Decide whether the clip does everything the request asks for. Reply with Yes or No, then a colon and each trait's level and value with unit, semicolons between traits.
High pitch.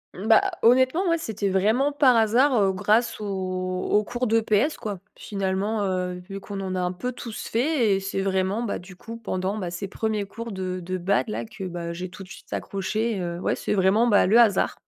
Yes: high, 200 Hz